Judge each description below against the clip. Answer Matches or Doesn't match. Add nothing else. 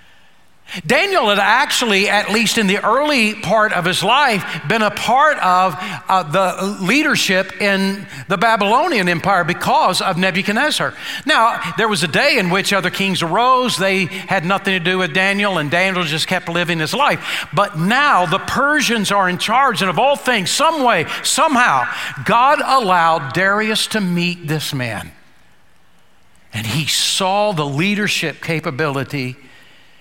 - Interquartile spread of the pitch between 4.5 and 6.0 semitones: Doesn't match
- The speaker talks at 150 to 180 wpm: Matches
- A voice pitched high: Matches